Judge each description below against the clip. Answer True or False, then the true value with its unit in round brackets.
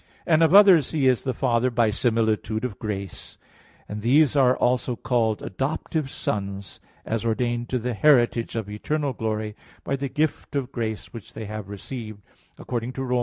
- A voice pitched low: True (120 Hz)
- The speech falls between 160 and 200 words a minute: True (170 wpm)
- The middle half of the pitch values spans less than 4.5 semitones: True (3.5 semitones)